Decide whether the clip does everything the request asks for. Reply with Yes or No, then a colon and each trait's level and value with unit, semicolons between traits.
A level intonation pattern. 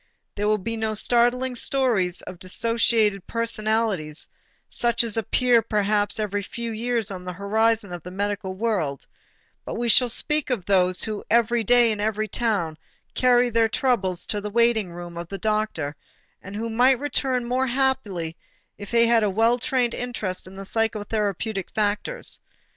No: average, 3.1 semitones